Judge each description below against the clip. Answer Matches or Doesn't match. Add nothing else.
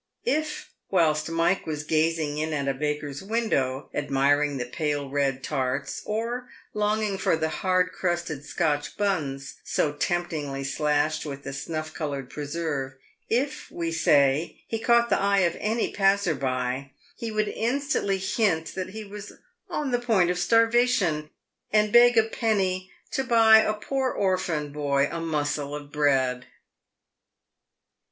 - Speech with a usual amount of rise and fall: Doesn't match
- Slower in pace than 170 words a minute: Matches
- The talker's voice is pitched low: Doesn't match